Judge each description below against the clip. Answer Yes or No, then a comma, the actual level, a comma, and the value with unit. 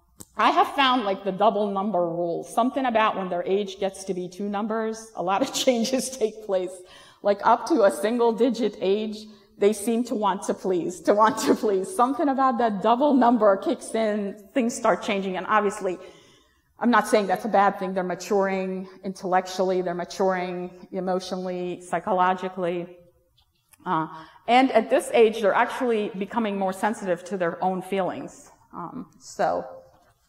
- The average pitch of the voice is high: Yes, high, 200 Hz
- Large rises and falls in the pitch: No, average, 3.5 semitones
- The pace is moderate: No, fast, 165 wpm